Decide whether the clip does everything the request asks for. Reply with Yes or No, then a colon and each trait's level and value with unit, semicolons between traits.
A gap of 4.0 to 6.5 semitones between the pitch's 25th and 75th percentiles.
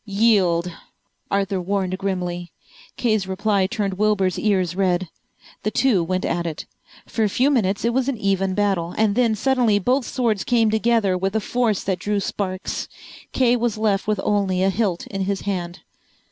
No: average, 2.8 semitones